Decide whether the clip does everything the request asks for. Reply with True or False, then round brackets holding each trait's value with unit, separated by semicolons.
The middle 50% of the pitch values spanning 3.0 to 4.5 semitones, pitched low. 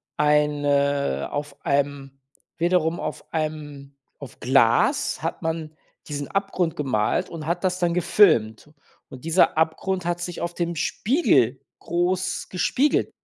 False (3.7 semitones; 155 Hz)